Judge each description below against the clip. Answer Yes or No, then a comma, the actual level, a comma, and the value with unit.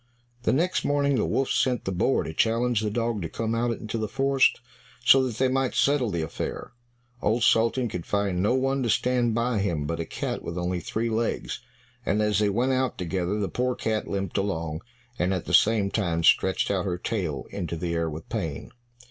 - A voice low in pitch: Yes, low, 110 Hz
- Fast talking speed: Yes, fast, 210 wpm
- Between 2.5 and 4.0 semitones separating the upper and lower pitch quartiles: No, wide, 5.4 semitones